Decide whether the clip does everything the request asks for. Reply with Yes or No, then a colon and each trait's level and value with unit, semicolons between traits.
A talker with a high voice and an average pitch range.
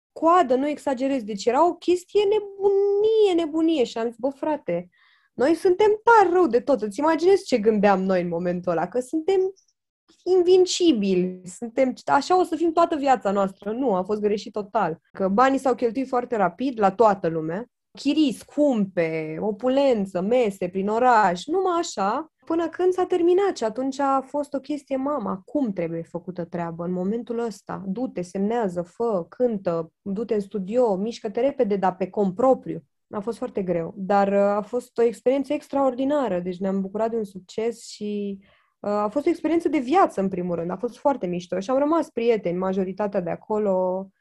No: high, 235 Hz; wide, 7.2 semitones